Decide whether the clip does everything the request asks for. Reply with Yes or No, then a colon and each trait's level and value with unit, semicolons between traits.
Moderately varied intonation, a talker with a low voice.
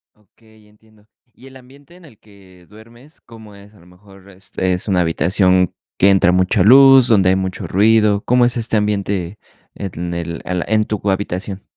Yes: average, 3.1 semitones; low, 100 Hz